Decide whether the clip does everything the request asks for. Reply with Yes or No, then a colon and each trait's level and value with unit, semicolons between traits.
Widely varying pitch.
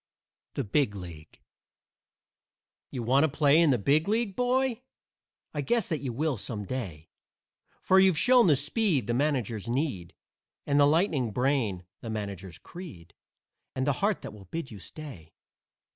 Yes: wide, 7.2 semitones